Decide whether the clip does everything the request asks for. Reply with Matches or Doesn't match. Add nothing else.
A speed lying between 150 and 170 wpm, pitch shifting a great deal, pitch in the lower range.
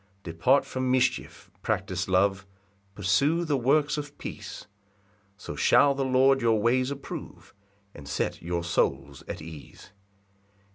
Doesn't match